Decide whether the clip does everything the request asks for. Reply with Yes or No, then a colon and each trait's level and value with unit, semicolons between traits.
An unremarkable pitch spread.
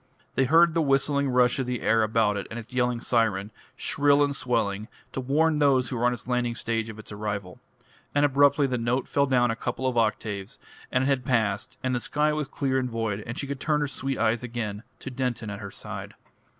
Yes: average, 3.5 semitones